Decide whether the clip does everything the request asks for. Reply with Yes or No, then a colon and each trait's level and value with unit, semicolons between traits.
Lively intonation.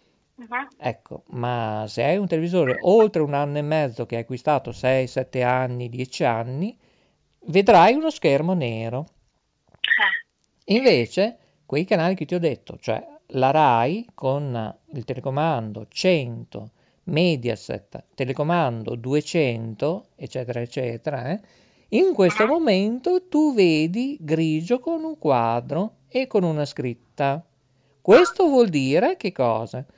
Yes: wide, 7.5 semitones